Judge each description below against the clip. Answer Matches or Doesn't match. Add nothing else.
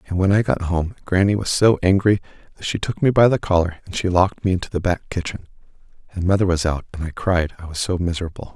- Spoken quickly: Matches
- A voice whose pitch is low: Matches